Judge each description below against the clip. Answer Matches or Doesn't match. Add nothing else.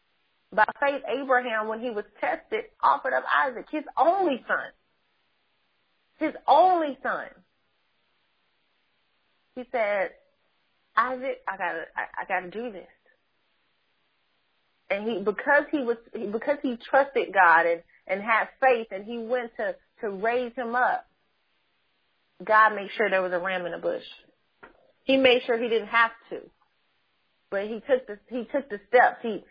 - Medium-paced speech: Matches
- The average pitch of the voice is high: Matches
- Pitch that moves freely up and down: Doesn't match